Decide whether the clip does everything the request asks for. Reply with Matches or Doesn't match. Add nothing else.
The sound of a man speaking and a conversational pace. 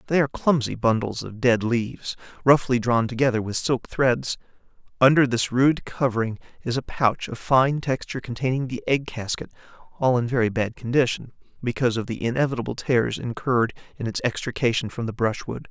Matches